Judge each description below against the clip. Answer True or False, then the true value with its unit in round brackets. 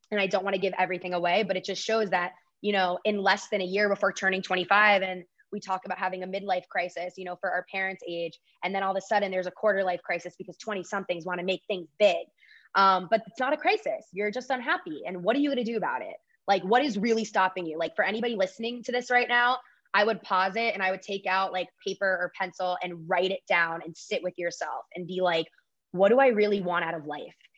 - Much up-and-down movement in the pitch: False (2.7 semitones)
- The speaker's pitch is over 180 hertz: True (190 Hz)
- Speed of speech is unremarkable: False (255 wpm)